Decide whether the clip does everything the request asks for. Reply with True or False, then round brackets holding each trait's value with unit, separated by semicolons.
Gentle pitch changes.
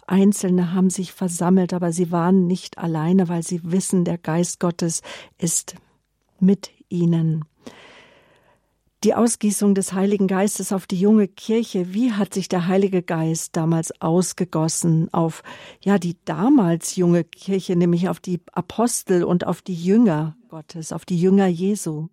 True (2.3 semitones)